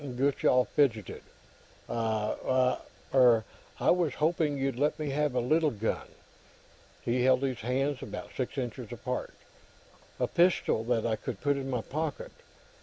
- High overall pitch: No, low, 130 Hz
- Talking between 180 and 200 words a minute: No, average, 145 wpm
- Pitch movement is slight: No, average, 3.2 semitones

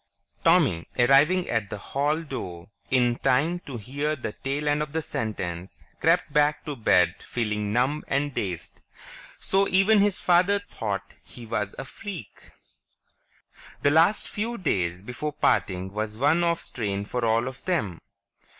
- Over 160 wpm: No, average, 150 wpm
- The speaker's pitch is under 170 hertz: Yes, low, 135 Hz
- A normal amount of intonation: No, wide, 7.2 semitones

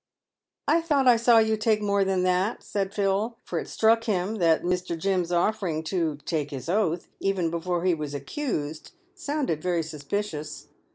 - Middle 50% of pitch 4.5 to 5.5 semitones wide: Yes, average, 4.8 semitones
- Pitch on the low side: No, medium, 185 Hz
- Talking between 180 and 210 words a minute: No, average, 170 wpm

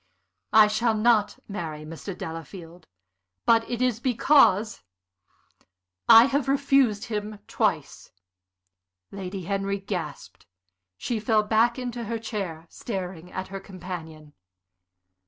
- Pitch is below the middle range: No, high, 210 Hz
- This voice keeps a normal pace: No, slow, 110 wpm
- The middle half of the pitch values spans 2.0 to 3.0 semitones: No, average, 4.1 semitones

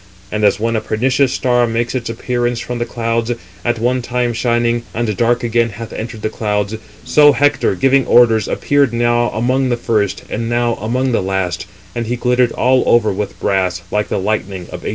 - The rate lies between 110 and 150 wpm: No, fast, 205 wpm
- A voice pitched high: No, low, 120 Hz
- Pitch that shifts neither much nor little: No, narrow, 2.1 semitones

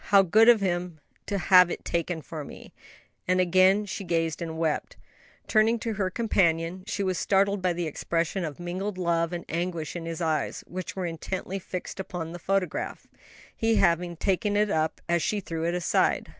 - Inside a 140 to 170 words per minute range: No, average, 190 wpm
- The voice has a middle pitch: Yes, medium, 180 Hz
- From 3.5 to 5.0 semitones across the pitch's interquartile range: No, average, 2.8 semitones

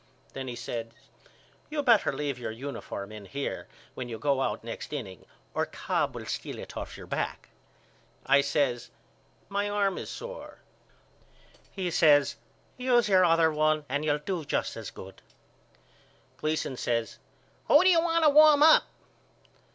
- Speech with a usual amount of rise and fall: No, wide, 8.6 semitones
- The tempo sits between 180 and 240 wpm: No, average, 155 wpm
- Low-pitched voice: No, medium, 150 Hz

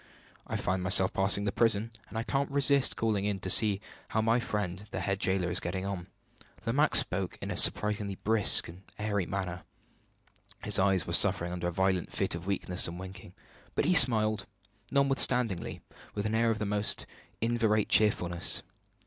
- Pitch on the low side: Yes, low, 100 Hz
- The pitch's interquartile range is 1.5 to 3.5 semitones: Yes, average, 3.2 semitones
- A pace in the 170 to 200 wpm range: Yes, average, 175 wpm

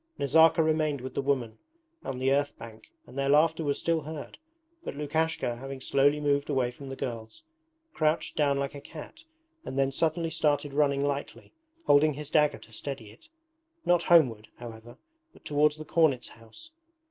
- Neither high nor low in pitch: Yes, medium, 145 Hz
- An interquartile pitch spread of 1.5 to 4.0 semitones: Yes, average, 2.8 semitones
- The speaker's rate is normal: Yes, average, 170 wpm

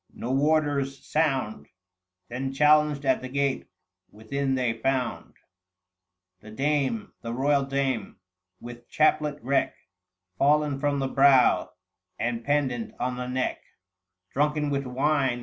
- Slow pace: Yes, slow, 120 wpm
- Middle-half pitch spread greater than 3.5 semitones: No, narrow, 2.4 semitones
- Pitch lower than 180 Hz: Yes, low, 135 Hz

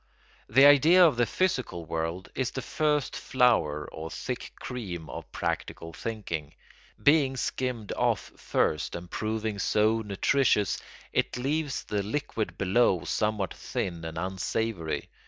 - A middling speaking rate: No, slow, 130 wpm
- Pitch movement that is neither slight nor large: No, wide, 6.7 semitones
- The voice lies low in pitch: Yes, low, 110 Hz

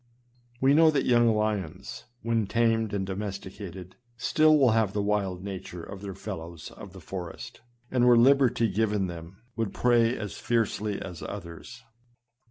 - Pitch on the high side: No, low, 105 Hz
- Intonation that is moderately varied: Yes, average, 3.6 semitones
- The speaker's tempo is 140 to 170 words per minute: Yes, average, 155 wpm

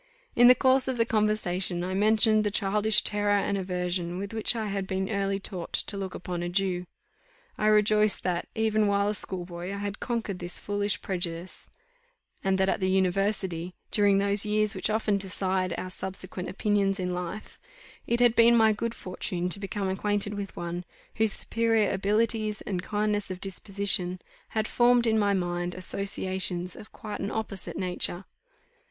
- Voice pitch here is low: No, high, 200 Hz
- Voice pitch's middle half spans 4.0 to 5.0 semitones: No, narrow, 2.5 semitones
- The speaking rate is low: No, average, 170 wpm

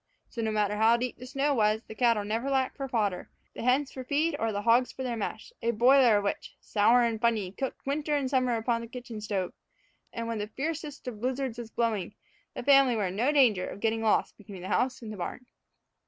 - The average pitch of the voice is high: Yes, high, 235 Hz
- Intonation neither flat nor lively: Yes, average, 3.4 semitones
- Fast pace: Yes, fast, 230 wpm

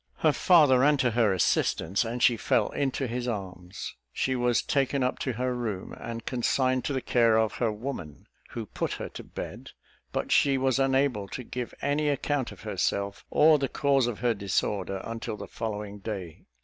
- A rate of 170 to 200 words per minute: Yes, average, 190 wpm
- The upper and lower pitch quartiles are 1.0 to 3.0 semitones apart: No, average, 4.1 semitones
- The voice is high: No, low, 120 Hz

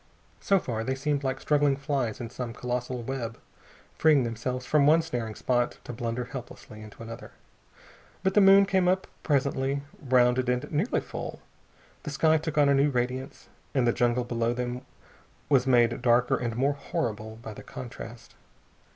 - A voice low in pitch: Yes, low, 125 Hz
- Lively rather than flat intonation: No, average, 3.0 semitones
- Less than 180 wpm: Yes, average, 170 wpm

